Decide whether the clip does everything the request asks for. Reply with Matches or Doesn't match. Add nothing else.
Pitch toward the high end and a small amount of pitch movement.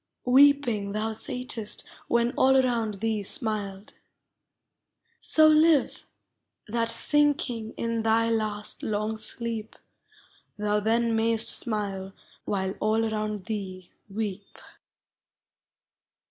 Matches